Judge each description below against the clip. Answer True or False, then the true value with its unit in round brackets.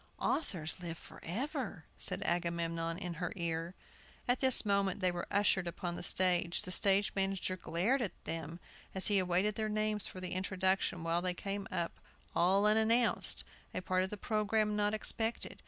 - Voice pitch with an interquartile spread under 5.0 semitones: True (3.3 semitones)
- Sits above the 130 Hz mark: True (190 Hz)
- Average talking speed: True (165 wpm)